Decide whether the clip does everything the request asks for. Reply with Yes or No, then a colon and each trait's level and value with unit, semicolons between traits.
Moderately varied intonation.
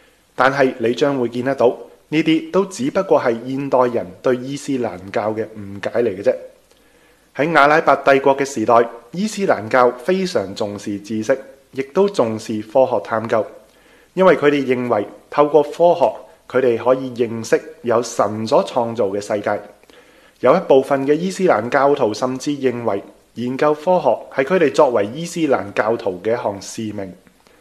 Yes: average, 4.6 semitones